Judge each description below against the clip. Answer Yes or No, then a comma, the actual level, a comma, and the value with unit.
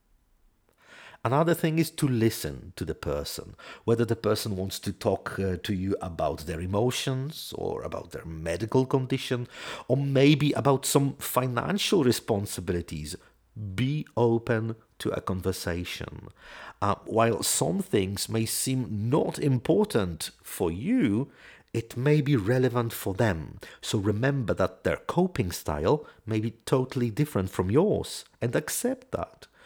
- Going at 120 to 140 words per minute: Yes, slow, 135 wpm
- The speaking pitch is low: Yes, low, 120 Hz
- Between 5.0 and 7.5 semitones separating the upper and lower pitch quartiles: Yes, wide, 5.6 semitones